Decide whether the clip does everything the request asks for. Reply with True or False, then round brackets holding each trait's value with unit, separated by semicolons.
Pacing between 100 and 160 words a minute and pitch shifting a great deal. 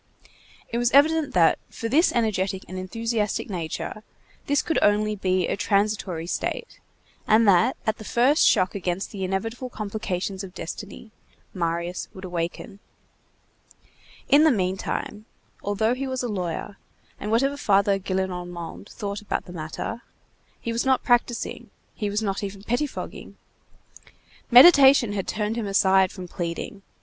False (140 wpm; 3.7 semitones)